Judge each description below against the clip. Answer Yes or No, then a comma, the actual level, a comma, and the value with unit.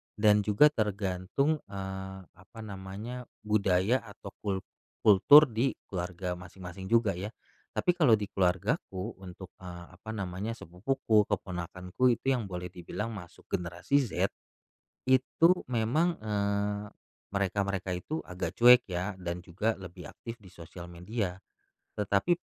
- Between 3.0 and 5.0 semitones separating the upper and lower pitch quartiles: Yes, average, 3.7 semitones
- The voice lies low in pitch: Yes, low, 100 Hz